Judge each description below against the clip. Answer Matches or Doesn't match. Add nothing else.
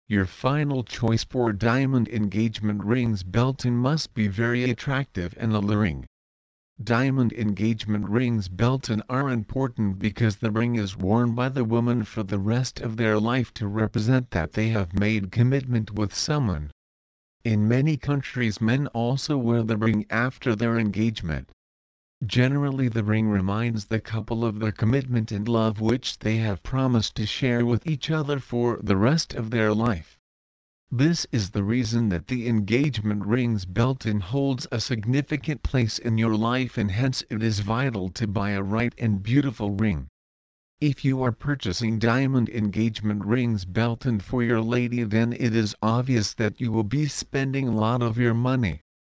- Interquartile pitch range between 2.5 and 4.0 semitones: Matches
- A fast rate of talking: Doesn't match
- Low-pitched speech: Matches